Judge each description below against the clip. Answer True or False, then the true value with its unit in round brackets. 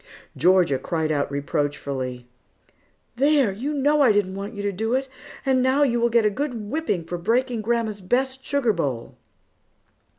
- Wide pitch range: True (7.1 semitones)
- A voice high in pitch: True (215 Hz)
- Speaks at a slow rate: False (165 wpm)